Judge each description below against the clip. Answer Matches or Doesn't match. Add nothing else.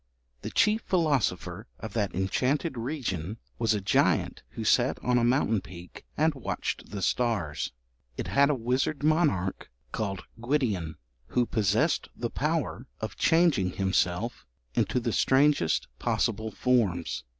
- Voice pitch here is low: Matches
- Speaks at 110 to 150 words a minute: Matches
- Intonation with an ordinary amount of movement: Doesn't match